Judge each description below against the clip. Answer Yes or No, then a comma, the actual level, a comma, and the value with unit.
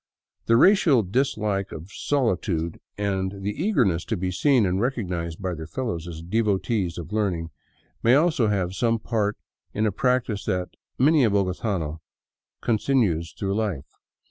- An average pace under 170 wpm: Yes, average, 145 wpm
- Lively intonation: No, average, 4.5 semitones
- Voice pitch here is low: Yes, low, 100 Hz